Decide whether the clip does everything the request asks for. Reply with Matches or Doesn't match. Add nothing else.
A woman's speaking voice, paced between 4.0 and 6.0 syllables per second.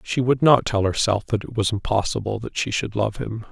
Doesn't match